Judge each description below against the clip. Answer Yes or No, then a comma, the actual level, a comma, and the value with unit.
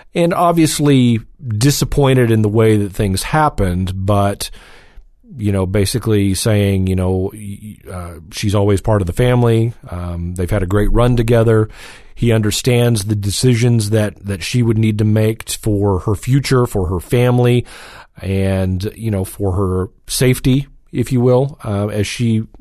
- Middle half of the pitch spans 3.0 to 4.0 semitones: Yes, average, 3.7 semitones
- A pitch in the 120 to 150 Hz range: No, low, 110 Hz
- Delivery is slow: No, average, 155 wpm